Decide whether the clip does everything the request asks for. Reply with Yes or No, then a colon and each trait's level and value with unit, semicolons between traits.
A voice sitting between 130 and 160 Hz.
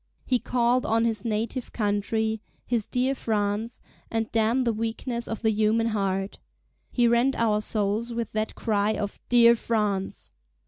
No: high, 225 Hz